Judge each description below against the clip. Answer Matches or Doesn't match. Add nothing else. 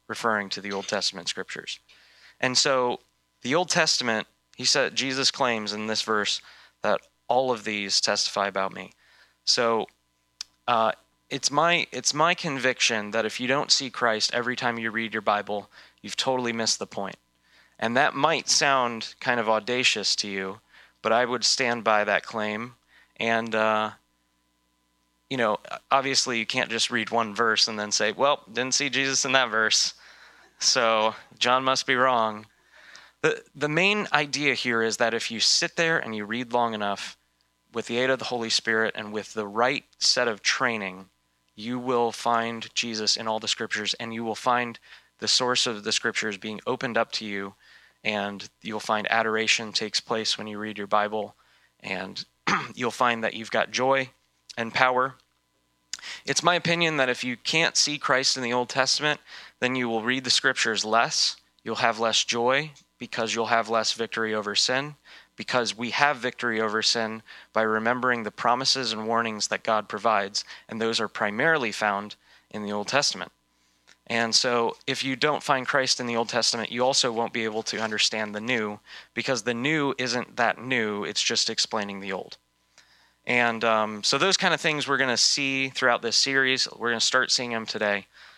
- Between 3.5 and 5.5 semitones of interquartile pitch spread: Doesn't match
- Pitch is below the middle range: Matches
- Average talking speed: Matches